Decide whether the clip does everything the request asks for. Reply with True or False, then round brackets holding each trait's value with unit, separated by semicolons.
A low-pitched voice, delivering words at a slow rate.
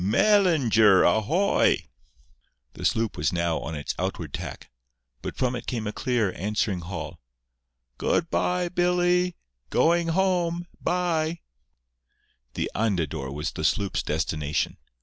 True (120 Hz; 130 wpm)